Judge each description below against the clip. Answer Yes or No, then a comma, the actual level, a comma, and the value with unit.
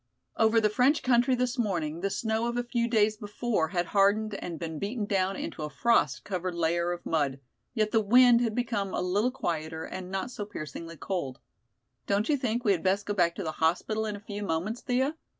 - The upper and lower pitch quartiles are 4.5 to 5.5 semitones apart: Yes, average, 5.1 semitones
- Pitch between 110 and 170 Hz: No, high, 205 Hz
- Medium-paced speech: No, fast, 215 wpm